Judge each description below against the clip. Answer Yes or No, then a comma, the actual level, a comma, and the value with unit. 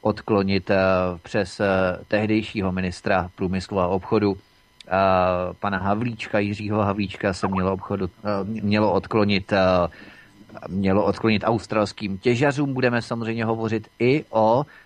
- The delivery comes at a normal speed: No, slow, 100 wpm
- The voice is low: Yes, low, 100 Hz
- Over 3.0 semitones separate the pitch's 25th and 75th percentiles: No, narrow, 2.4 semitones